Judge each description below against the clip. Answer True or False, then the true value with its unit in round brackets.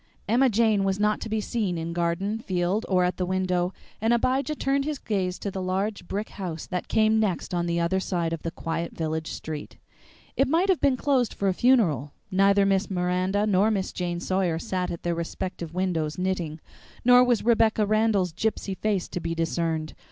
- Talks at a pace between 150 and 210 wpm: True (195 wpm)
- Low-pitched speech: False (190 Hz)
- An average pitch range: True (4.0 semitones)